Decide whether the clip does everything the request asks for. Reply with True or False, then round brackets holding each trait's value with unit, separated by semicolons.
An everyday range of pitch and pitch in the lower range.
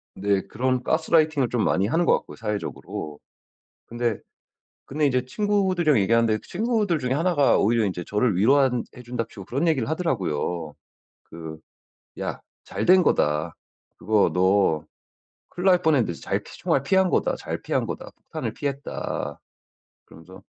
False (8.2 semitones; 125 Hz)